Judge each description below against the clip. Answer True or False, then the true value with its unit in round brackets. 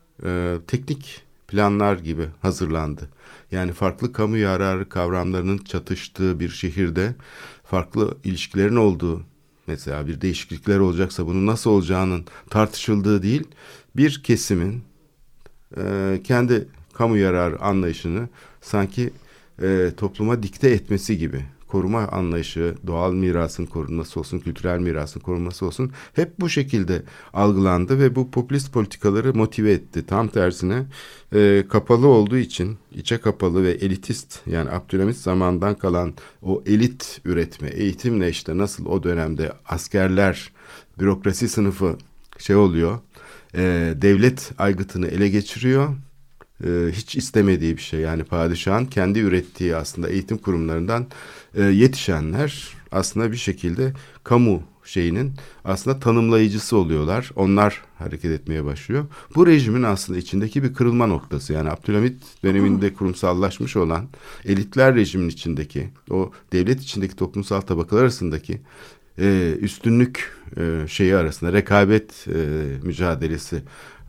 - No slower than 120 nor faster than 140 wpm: False (110 wpm)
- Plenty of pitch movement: False (4.4 semitones)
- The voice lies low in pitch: True (95 Hz)